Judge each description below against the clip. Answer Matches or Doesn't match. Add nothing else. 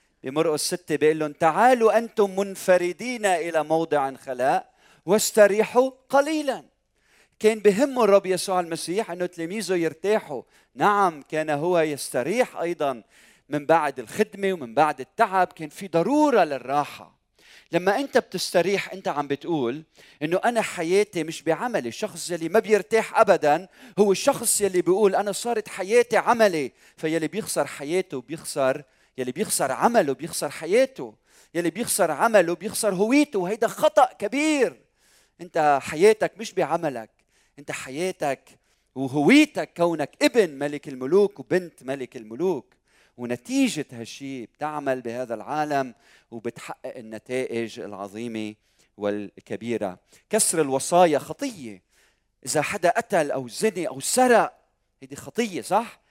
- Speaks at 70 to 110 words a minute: Doesn't match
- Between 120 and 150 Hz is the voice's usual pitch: Doesn't match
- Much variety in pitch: Matches